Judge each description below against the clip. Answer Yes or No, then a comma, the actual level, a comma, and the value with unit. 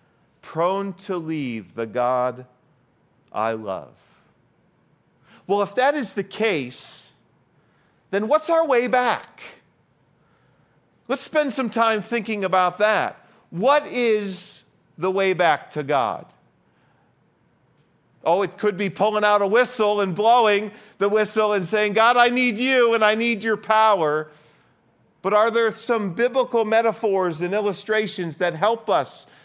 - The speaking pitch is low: No, high, 210 Hz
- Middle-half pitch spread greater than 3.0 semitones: Yes, average, 4.7 semitones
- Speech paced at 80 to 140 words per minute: Yes, slow, 135 wpm